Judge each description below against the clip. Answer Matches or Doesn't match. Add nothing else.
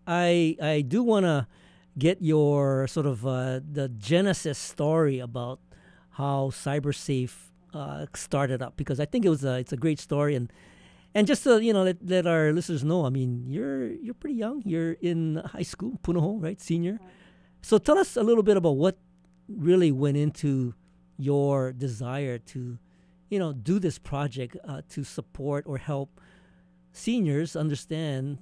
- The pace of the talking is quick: Doesn't match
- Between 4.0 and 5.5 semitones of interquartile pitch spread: Matches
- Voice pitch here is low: Doesn't match